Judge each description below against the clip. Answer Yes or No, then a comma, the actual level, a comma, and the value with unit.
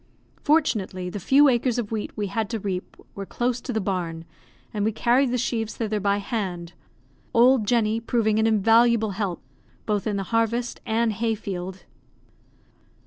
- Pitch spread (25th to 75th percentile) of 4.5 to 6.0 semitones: No, average, 2.8 semitones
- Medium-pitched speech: No, high, 220 Hz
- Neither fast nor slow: Yes, average, 165 wpm